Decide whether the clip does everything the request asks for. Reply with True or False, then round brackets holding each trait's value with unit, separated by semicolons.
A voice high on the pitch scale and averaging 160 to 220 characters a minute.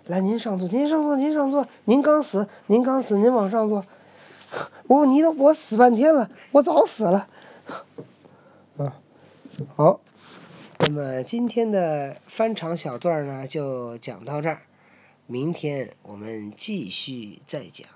True (200 Hz; 195 characters per minute)